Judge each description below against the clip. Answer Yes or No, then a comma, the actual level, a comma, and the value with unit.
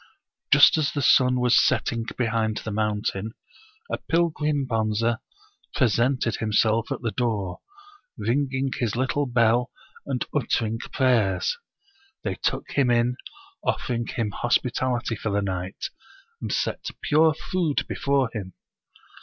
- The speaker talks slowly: Yes, slow, 130 wpm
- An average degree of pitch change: Yes, average, 3.3 semitones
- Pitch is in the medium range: No, low, 120 Hz